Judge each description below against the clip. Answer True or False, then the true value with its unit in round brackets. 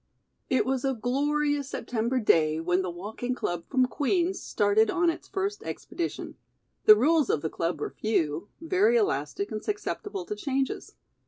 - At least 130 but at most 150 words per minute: False (160 wpm)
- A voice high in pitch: True (265 Hz)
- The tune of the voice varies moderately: False (8.5 semitones)